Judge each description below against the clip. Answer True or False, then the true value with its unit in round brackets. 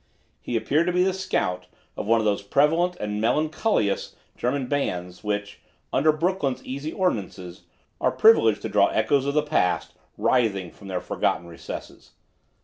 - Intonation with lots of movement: True (7.7 semitones)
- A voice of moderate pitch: False (130 Hz)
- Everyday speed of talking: True (155 wpm)